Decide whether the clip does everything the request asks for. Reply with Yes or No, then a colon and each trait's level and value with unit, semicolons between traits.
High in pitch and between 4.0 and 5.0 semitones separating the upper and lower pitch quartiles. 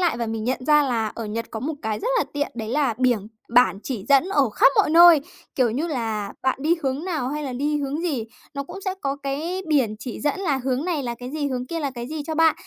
Yes: very high, 275 Hz; average, 4.3 semitones